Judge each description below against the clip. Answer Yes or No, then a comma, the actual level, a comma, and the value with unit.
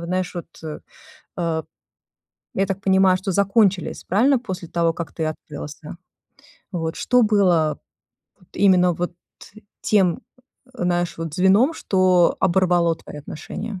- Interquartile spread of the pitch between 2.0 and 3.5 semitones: Yes, narrow, 2.5 semitones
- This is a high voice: No, medium, 180 Hz